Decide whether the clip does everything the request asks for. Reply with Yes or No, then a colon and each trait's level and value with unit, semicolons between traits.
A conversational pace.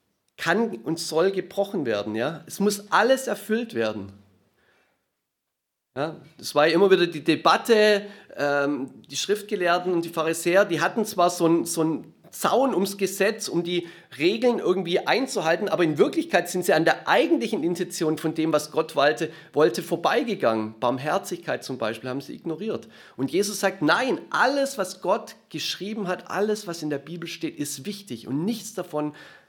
Yes: average, 165 wpm